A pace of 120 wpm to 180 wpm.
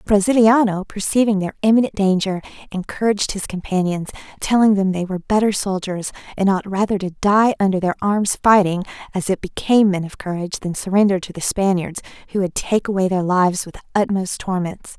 Yes: average, 175 wpm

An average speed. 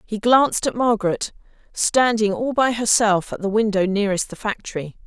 Yes: average, 165 wpm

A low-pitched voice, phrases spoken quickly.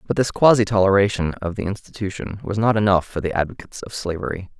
No: low, 100 Hz; average, 195 wpm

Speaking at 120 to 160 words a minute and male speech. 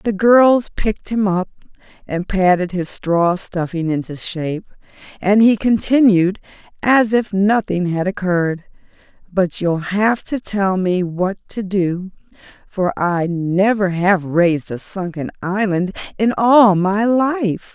No: average, 140 wpm; female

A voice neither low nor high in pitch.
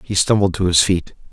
No: very low, 90 Hz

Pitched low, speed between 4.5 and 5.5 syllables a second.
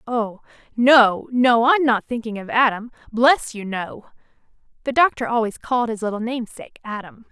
No: high, 235 Hz; 5.0 syllables/s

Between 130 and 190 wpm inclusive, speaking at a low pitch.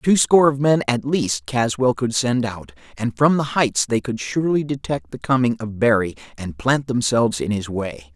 No: fast, 205 wpm; low, 120 Hz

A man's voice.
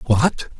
Yes: male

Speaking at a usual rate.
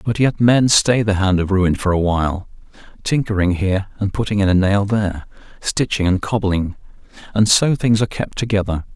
Yes: average, 190 wpm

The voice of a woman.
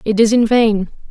Yes: female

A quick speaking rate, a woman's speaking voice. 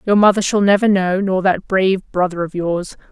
Yes: fast, 210 wpm; female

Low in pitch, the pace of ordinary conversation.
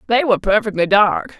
No: high, 210 Hz; average, 175 wpm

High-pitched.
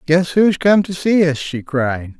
No: medium, 160 Hz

